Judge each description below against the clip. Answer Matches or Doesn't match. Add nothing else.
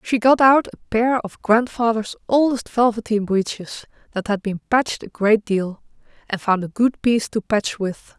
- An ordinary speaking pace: Matches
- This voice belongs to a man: Doesn't match